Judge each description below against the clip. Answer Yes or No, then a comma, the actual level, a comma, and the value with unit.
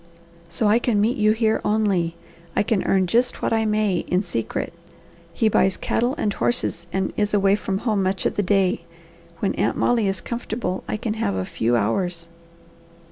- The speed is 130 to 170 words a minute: No, average, 190 wpm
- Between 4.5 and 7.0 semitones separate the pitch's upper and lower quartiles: No, average, 3.3 semitones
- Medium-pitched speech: No, high, 205 Hz